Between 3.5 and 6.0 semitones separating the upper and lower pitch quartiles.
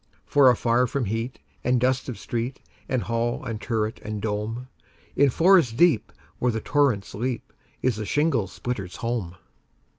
No: average, 2.8 semitones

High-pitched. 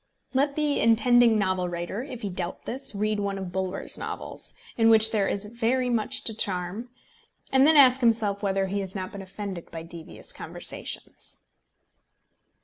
Yes: high, 210 Hz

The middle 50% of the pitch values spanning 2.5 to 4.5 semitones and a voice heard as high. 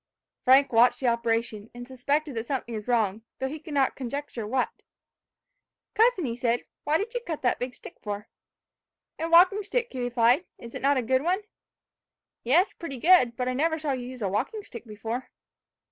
No: average, 4.9 semitones; very high, 255 Hz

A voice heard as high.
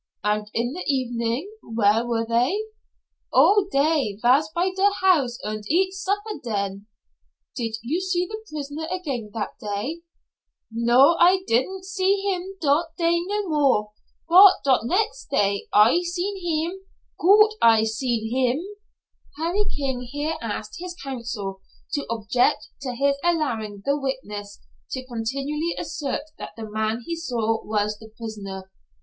Yes: very high, 270 Hz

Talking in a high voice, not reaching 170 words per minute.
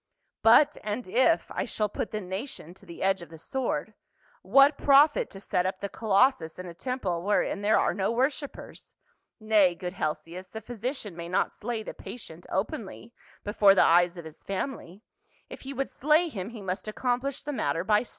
No: high, 210 Hz; average, 190 wpm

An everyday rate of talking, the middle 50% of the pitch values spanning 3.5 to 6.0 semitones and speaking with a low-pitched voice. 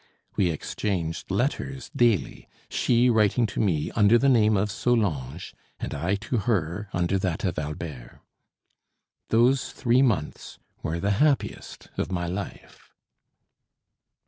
No: slow, 125 wpm; wide, 5.6 semitones; low, 100 Hz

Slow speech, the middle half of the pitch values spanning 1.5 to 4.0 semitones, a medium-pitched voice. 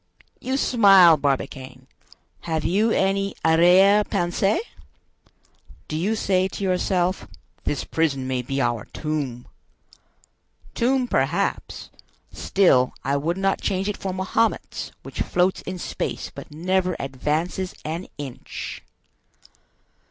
No: slow, 115 wpm; average, 5.1 semitones; medium, 175 Hz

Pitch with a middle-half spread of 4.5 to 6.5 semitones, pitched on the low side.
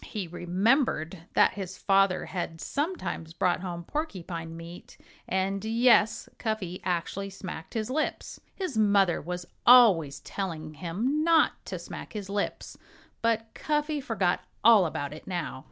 No: average, 4.8 semitones; high, 195 Hz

